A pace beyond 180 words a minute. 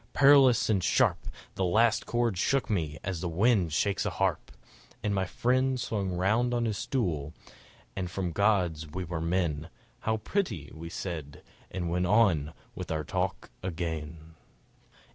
No: average, 150 wpm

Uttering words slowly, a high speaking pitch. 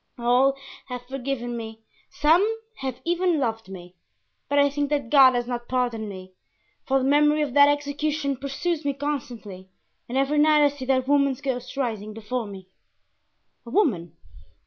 No: average, 165 wpm; very high, 265 Hz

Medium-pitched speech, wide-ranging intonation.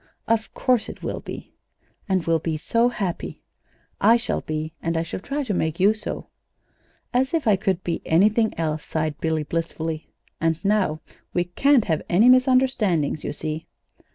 Yes: medium, 180 Hz; wide, 5.9 semitones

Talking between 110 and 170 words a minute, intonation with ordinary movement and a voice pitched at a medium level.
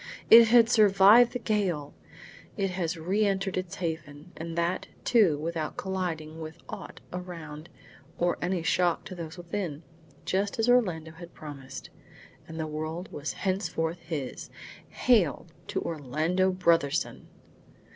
Yes: slow, 135 wpm; average, 3.4 semitones; medium, 175 Hz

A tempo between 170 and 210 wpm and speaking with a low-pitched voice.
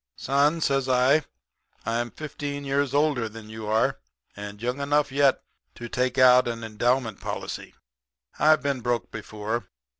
No: average, 145 wpm; low, 125 Hz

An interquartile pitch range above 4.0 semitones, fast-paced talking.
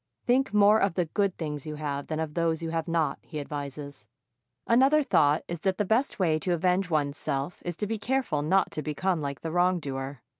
Yes: average, 4.5 semitones; fast, 215 wpm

